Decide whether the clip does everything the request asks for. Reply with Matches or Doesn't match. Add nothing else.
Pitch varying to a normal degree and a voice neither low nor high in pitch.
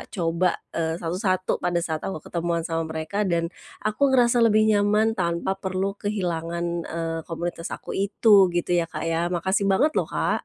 Matches